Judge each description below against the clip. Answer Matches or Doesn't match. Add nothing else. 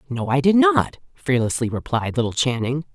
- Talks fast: Doesn't match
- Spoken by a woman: Matches